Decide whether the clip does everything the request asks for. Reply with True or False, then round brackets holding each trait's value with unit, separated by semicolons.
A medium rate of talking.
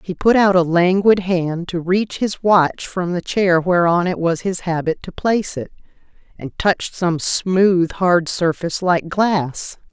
True (175 wpm)